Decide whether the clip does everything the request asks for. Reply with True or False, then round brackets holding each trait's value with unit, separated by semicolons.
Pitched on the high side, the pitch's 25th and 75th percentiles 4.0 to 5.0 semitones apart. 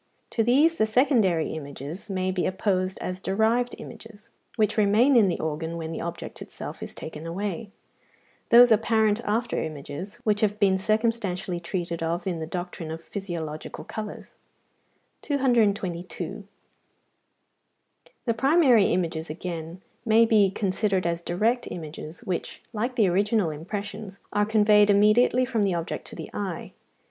True (200 Hz; 4.4 semitones)